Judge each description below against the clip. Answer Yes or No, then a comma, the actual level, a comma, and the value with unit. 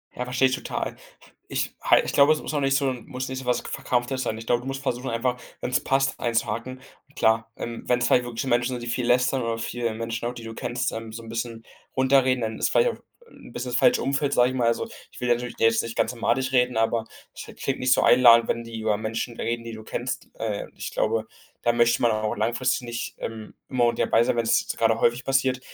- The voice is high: No, low, 120 Hz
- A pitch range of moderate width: No, narrow, 2.0 semitones